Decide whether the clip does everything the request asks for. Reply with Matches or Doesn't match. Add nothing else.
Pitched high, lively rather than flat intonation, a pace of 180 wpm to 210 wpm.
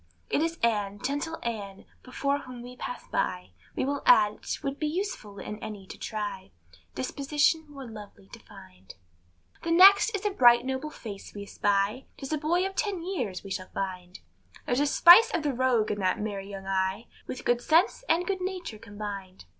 Matches